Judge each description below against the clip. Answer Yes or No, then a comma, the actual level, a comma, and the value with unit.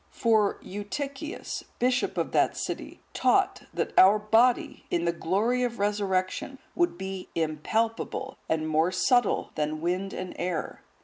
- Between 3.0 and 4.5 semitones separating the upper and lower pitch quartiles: No, wide, 5.4 semitones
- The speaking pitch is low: No, high, 200 Hz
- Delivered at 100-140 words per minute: Yes, slow, 135 wpm